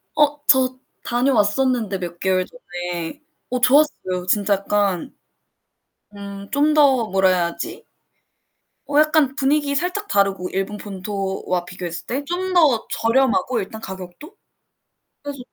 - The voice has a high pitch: Yes, high, 225 Hz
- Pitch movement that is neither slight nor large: No, wide, 6.9 semitones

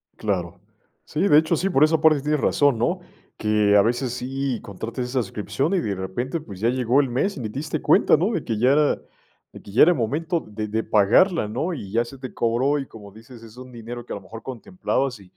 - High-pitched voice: No, low, 125 Hz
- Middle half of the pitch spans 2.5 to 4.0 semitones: No, average, 4.8 semitones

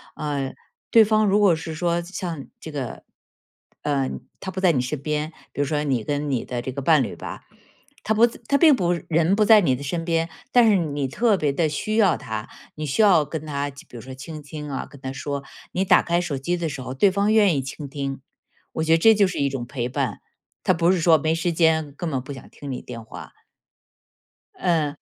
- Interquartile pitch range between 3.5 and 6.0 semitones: Yes, average, 4.4 semitones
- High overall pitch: No, medium, 155 Hz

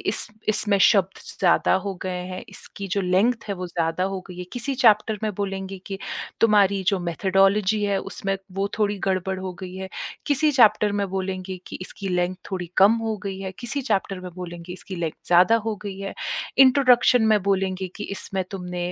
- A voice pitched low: No, high, 195 Hz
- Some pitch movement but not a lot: No, narrow, 2.1 semitones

